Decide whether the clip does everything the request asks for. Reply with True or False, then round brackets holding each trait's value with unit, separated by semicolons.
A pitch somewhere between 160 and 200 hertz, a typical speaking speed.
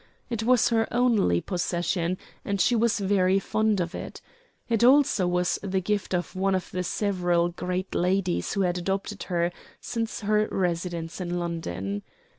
True (185 Hz; 160 wpm)